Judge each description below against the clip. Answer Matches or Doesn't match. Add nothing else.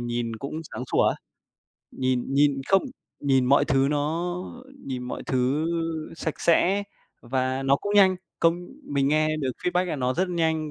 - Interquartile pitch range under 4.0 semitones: Doesn't match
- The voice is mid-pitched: Matches